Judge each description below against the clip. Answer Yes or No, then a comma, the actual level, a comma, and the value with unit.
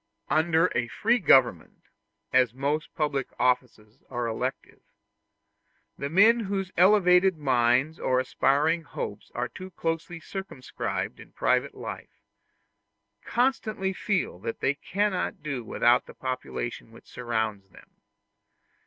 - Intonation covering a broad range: Yes, wide, 7.0 semitones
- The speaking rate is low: Yes, slow, 120 wpm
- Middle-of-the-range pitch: Yes, medium, 145 Hz